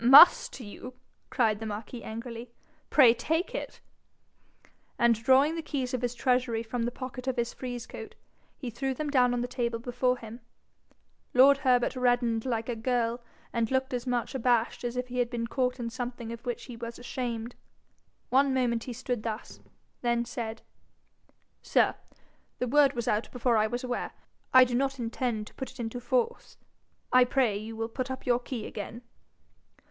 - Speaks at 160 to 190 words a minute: Yes, average, 180 wpm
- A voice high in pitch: Yes, high, 245 Hz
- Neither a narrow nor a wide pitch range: No, narrow, 1.7 semitones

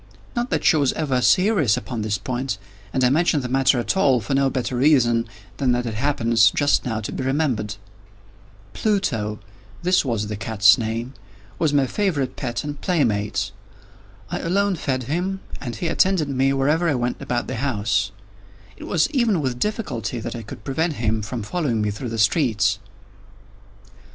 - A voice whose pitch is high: No, low, 130 Hz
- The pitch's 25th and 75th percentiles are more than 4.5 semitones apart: Yes, average, 5.2 semitones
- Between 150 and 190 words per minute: Yes, average, 170 wpm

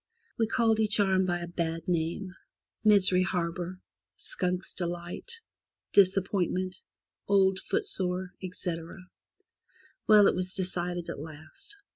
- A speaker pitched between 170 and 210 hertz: Yes, medium, 185 Hz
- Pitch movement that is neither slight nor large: No, narrow, 2.1 semitones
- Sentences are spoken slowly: Yes, slow, 115 wpm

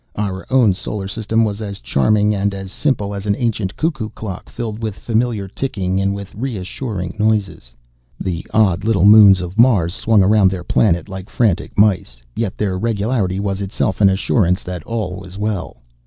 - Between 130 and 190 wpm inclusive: Yes, average, 175 wpm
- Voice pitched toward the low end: Yes, low, 100 Hz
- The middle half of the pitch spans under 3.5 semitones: Yes, narrow, 2.6 semitones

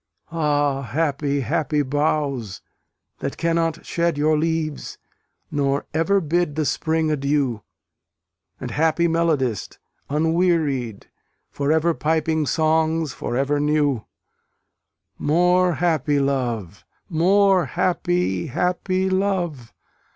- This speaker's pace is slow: Yes, slow, 100 wpm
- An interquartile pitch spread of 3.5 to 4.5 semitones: No, average, 3.1 semitones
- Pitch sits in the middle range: Yes, medium, 155 Hz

